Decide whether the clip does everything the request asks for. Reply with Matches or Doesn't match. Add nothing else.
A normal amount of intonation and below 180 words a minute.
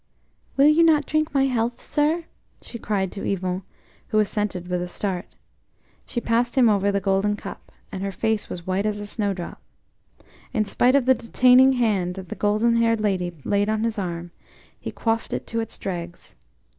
Doesn't match